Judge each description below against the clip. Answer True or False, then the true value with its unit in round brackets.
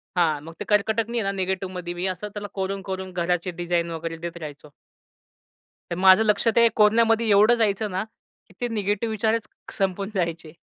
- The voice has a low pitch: False (190 Hz)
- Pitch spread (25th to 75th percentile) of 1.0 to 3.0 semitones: False (3.5 semitones)